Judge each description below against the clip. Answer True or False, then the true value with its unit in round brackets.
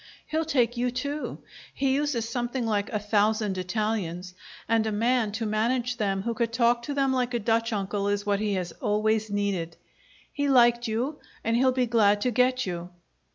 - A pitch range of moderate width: True (3.2 semitones)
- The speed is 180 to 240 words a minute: True (190 wpm)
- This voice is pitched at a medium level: False (230 Hz)